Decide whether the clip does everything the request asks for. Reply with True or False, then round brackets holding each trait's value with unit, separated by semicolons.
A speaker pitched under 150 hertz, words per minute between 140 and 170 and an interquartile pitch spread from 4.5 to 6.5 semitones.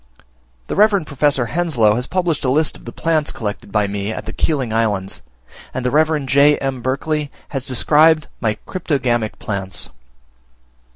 True (135 Hz; 160 wpm; 5.4 semitones)